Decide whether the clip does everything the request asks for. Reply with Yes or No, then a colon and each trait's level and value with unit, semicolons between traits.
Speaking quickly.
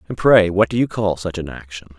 Yes: fast, 270 wpm